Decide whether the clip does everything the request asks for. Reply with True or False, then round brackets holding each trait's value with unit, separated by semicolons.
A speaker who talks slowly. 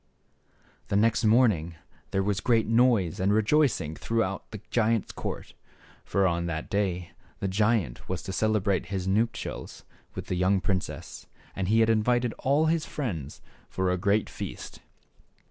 False (150 wpm)